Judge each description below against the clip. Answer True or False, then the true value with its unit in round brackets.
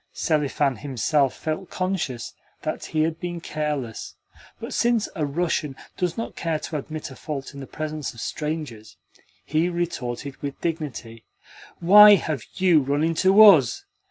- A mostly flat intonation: False (3.7 semitones)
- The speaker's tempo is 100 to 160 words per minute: True (150 wpm)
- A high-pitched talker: False (155 Hz)